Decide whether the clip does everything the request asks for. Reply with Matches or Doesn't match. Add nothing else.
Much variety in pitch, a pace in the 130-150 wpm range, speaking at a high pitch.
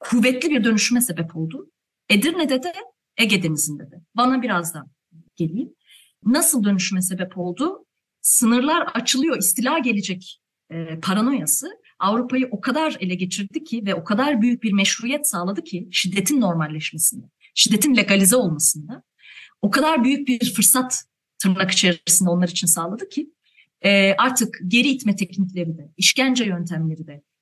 Matches